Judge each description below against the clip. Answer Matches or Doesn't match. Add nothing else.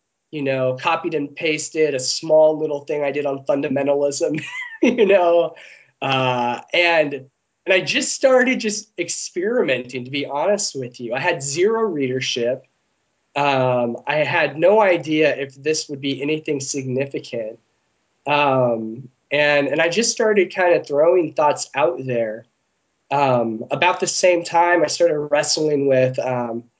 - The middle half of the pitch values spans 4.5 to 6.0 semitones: Matches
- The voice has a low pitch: Doesn't match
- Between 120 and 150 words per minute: Matches